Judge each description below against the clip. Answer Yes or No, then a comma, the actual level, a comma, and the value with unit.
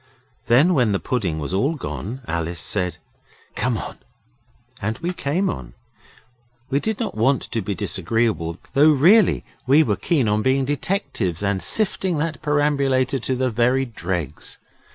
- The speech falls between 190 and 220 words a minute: No, average, 155 wpm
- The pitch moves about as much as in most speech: No, wide, 6.7 semitones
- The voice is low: Yes, low, 130 Hz